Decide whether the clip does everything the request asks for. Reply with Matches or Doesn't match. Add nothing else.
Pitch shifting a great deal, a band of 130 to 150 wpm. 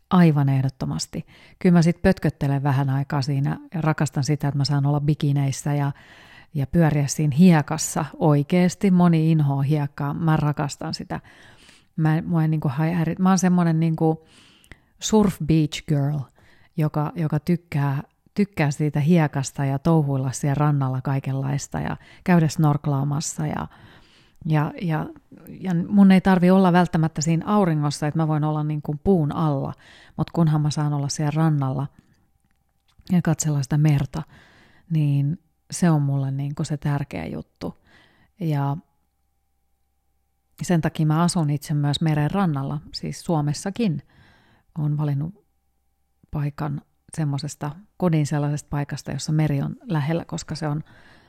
Doesn't match